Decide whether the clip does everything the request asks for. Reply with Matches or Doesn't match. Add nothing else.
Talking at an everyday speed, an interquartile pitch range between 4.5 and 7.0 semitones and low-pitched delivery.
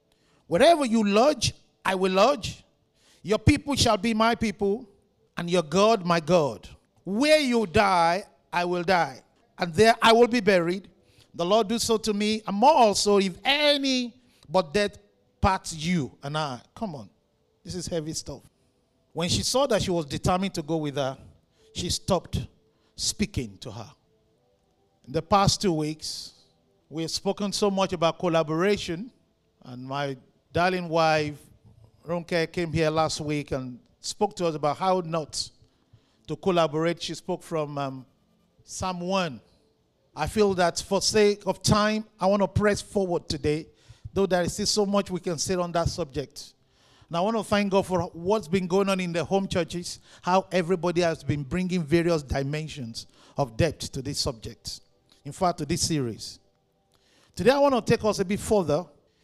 Doesn't match